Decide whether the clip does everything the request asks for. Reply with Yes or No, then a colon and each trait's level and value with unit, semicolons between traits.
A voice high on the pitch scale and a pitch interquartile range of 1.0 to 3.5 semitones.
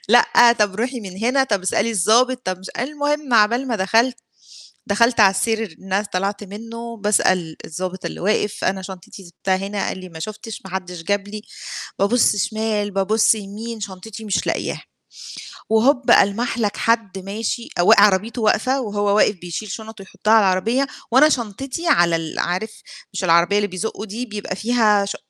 Yes: high, 210 Hz; average, 3.2 semitones